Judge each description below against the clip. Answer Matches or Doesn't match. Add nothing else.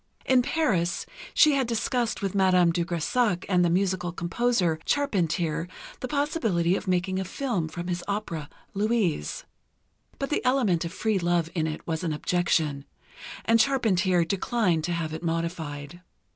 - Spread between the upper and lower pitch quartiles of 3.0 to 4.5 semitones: Doesn't match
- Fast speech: Doesn't match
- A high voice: Doesn't match